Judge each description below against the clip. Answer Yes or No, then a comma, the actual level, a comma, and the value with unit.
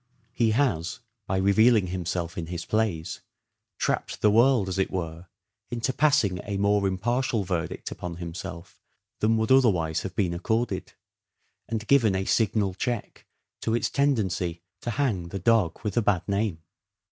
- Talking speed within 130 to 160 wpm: Yes, average, 155 wpm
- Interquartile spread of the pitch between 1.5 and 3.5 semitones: No, average, 4.3 semitones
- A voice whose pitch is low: Yes, low, 100 Hz